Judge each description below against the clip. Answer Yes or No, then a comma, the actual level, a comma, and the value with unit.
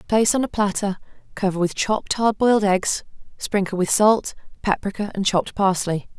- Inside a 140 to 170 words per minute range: Yes, average, 165 wpm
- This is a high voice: Yes, high, 200 Hz